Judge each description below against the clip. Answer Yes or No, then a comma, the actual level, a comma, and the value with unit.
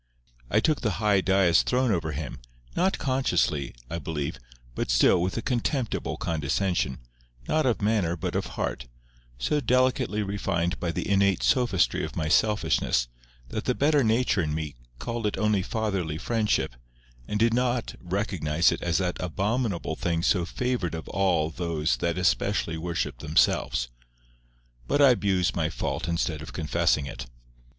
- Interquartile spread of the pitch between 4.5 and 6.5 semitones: Yes, wide, 5.6 semitones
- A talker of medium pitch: No, very low, 95 Hz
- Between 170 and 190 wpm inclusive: No, average, 155 wpm